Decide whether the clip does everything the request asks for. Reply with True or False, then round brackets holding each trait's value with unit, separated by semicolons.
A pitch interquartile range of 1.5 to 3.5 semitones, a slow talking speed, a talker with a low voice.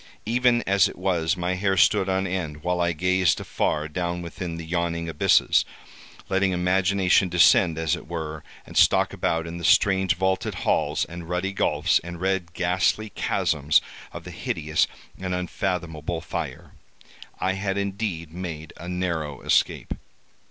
False (2.4 semitones; 150 wpm; 90 Hz)